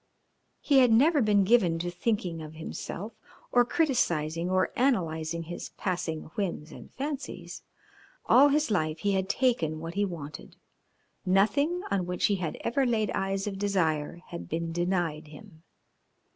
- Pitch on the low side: No, medium, 185 Hz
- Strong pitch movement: Yes, wide, 5.8 semitones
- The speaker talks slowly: No, average, 150 wpm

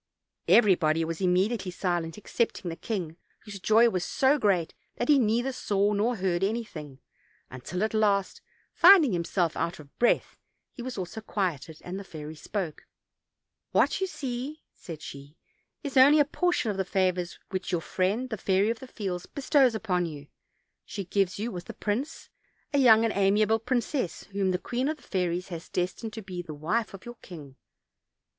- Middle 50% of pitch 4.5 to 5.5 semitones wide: Yes, average, 4.9 semitones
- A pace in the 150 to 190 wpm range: Yes, average, 180 wpm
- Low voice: No, high, 195 Hz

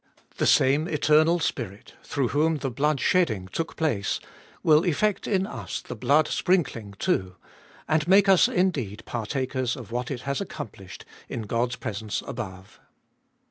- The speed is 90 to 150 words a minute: Yes, average, 145 wpm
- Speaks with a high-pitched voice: No, low, 135 Hz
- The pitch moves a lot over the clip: Yes, wide, 6.2 semitones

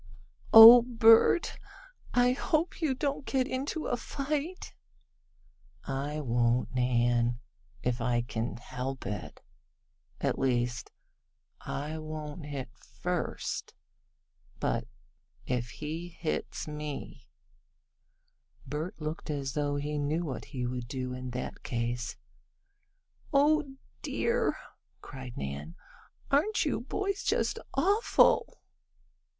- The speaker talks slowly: Yes, slow, 105 wpm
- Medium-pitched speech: Yes, medium, 150 Hz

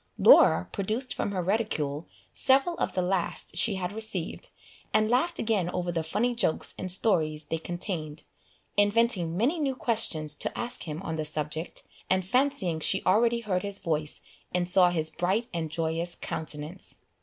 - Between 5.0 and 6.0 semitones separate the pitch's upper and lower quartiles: Yes, wide, 5.5 semitones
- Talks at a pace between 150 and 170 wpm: Yes, average, 165 wpm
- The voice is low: No, medium, 185 Hz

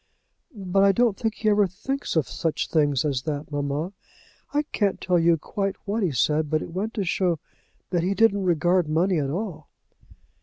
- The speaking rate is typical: Yes, average, 190 wpm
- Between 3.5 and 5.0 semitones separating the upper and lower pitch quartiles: Yes, average, 4.4 semitones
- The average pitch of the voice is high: No, medium, 180 Hz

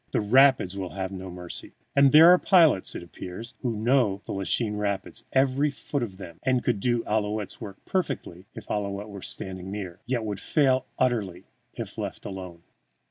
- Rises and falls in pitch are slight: No, average, 5.2 semitones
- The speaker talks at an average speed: Yes, average, 180 wpm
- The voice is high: No, low, 105 Hz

